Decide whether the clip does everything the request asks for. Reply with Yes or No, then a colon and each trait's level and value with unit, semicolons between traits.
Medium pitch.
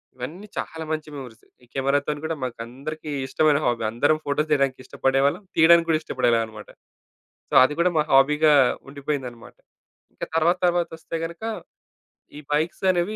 Yes: medium, 150 Hz